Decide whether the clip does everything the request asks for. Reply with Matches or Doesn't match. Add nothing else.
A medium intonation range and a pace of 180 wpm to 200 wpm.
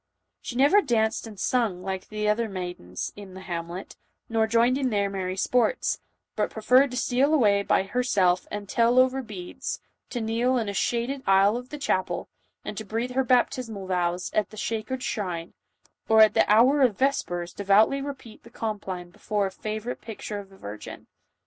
Matches